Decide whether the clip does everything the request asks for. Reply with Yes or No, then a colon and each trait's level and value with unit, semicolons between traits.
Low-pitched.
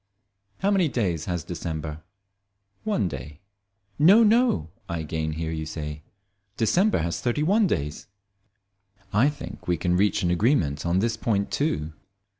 Yes: very low, 90 Hz